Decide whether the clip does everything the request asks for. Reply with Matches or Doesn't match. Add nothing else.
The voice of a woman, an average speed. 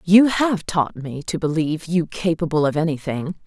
Matches